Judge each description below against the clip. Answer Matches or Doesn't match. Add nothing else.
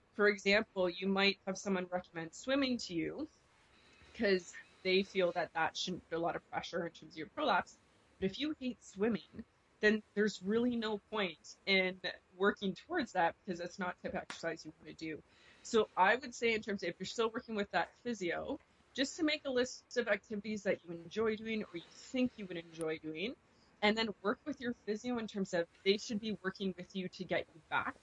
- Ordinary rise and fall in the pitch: Matches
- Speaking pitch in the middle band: Doesn't match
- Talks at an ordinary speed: Doesn't match